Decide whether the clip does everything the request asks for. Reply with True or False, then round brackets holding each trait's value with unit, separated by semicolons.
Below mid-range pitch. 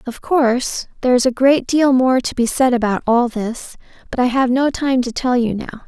False (250 Hz)